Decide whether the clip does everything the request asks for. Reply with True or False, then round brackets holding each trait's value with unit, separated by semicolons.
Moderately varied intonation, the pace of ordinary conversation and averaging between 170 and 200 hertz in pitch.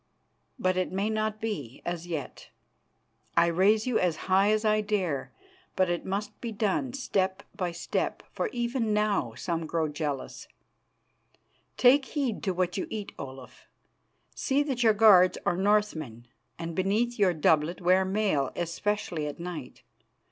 True (4.1 semitones; 150 wpm; 190 Hz)